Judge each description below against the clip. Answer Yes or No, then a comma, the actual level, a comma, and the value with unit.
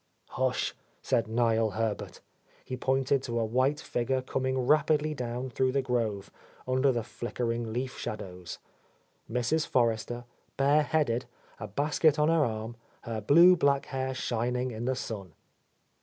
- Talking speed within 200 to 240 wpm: No, average, 140 wpm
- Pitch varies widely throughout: No, average, 3.1 semitones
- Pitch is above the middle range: No, low, 125 Hz